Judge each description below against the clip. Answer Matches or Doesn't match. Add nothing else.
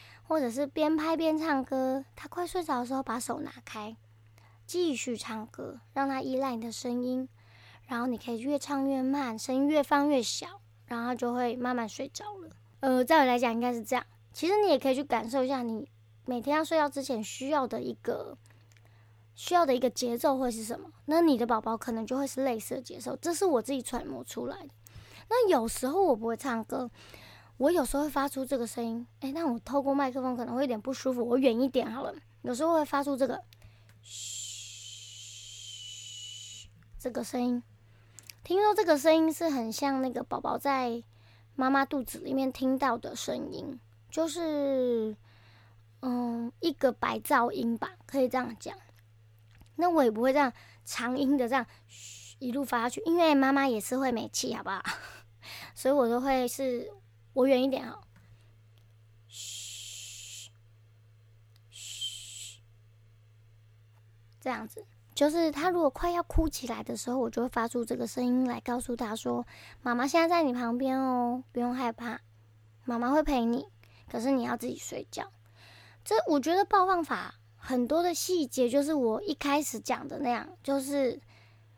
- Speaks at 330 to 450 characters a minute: Doesn't match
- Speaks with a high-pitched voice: Matches